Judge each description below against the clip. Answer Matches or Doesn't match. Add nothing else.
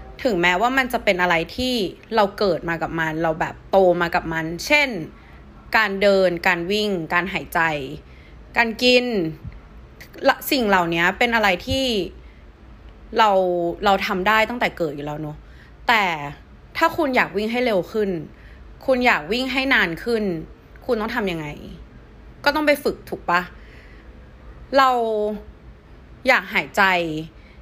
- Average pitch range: Doesn't match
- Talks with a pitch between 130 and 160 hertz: Doesn't match